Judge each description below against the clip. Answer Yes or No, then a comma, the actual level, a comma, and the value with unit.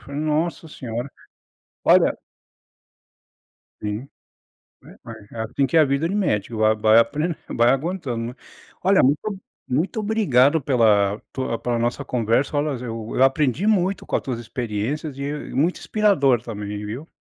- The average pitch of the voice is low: Yes, low, 130 Hz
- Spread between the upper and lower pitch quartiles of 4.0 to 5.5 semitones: Yes, average, 5.2 semitones